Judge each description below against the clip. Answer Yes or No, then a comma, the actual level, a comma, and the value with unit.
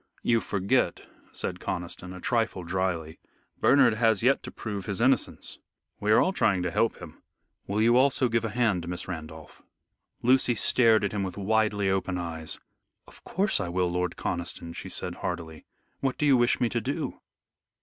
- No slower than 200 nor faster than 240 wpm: No, average, 180 wpm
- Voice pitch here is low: Yes, low, 100 Hz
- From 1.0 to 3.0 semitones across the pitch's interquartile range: No, average, 4.9 semitones